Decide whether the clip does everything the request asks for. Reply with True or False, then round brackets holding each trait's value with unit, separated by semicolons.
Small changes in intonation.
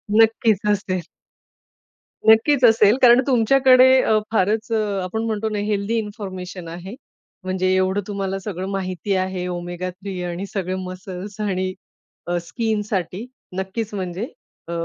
False (3.0 semitones)